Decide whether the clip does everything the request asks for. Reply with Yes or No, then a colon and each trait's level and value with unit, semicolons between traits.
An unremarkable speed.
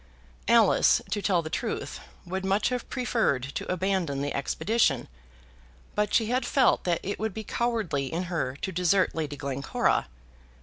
Yes: average, 160 wpm